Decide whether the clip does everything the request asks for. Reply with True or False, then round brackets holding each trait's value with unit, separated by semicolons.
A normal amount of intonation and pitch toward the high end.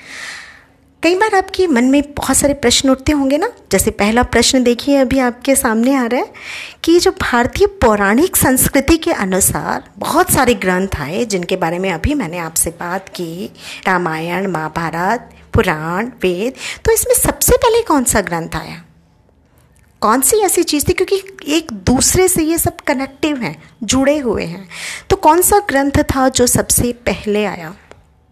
False (8.8 semitones; 260 Hz)